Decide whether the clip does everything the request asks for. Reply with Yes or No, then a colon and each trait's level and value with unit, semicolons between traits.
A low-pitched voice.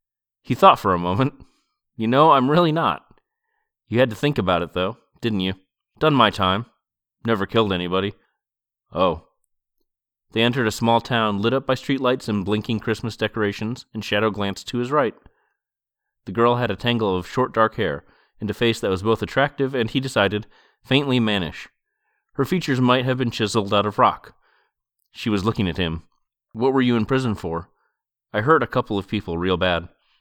Yes: low, 110 Hz